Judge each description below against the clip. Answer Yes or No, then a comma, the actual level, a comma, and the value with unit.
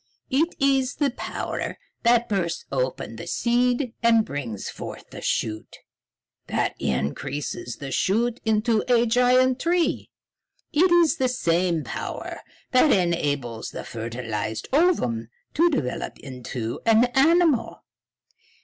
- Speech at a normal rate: No, slow, 120 wpm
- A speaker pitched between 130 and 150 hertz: No, high, 225 Hz